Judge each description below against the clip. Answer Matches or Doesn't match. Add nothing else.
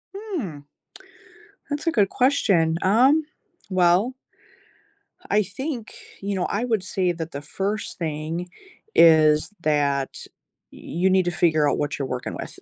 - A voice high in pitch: Doesn't match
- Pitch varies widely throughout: Matches